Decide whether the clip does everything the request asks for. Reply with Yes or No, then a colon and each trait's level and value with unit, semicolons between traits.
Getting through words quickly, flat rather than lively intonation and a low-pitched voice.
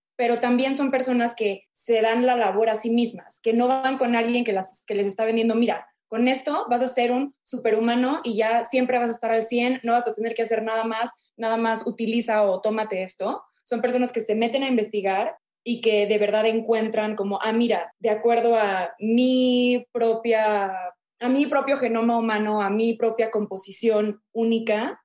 No: fast, 200 wpm; narrow, 1.9 semitones; high, 230 Hz